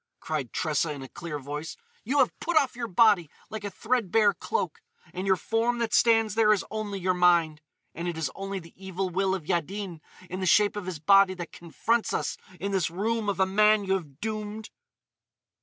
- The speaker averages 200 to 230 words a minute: Yes, fast, 205 wpm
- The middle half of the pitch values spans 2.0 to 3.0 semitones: No, average, 4.0 semitones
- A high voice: Yes, high, 195 Hz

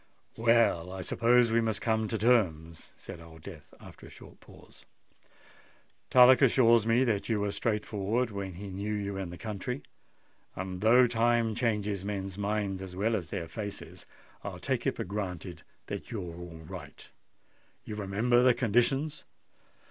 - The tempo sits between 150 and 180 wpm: Yes, average, 165 wpm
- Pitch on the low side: Yes, low, 105 Hz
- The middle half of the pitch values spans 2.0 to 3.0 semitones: No, average, 3.6 semitones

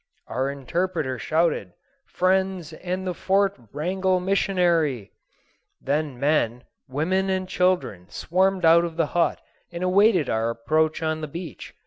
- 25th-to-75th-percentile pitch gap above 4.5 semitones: No, average, 4.2 semitones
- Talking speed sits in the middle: No, slow, 130 wpm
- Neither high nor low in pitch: Yes, medium, 170 Hz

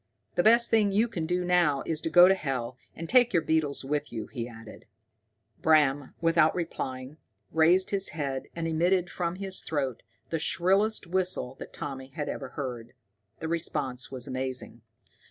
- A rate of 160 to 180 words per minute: Yes, average, 170 wpm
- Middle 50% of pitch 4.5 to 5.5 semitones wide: Yes, average, 5.1 semitones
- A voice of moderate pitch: Yes, medium, 160 Hz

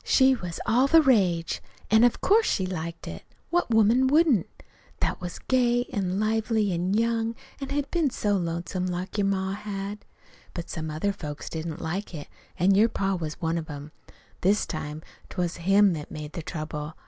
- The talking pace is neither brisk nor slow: Yes, average, 185 wpm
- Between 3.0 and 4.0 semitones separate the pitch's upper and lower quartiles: No, average, 5.1 semitones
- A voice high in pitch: Yes, high, 195 Hz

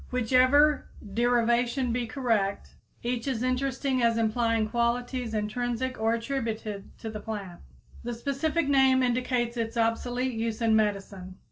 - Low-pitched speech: No, high, 235 Hz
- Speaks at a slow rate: Yes, slow, 130 wpm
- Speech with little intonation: Yes, narrow, 2.3 semitones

